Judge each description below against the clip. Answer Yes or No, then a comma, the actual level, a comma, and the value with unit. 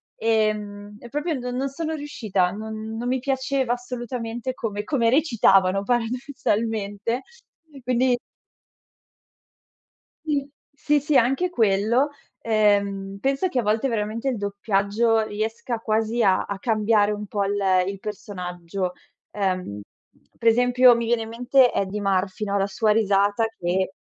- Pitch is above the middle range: Yes, high, 225 Hz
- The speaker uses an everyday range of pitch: Yes, average, 3.5 semitones